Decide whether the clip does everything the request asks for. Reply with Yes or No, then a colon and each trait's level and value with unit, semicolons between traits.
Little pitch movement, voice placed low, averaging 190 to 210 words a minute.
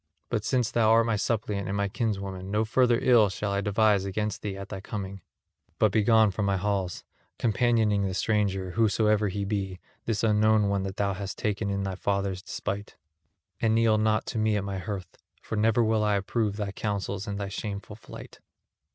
Yes: narrow, 1.8 semitones; low, 105 Hz; average, 195 wpm